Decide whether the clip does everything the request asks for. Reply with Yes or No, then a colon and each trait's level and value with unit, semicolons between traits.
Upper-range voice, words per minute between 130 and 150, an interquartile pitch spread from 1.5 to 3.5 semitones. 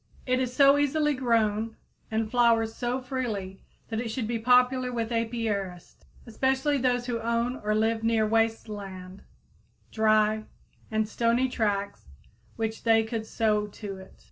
Yes: high, 225 Hz; average, 145 wpm; narrow, 2.4 semitones